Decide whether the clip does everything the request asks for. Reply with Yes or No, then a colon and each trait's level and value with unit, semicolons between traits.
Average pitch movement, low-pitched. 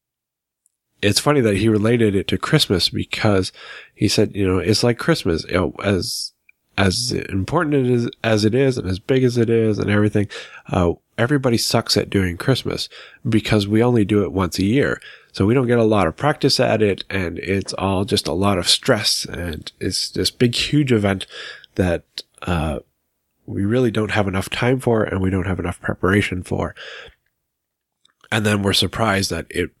Yes: average, 3.6 semitones; low, 105 Hz